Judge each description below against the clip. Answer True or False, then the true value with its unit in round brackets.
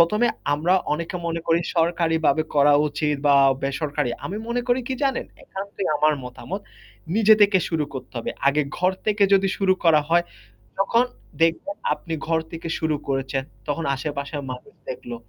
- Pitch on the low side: False (165 Hz)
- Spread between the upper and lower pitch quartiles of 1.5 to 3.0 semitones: False (5.0 semitones)